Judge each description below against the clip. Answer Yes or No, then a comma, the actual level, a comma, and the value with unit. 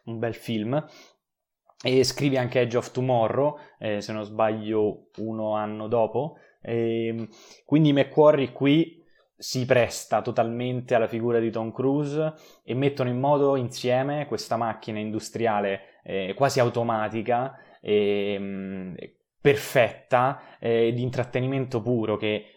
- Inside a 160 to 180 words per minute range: No, average, 125 wpm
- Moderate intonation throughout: Yes, average, 3.4 semitones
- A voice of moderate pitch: No, low, 120 Hz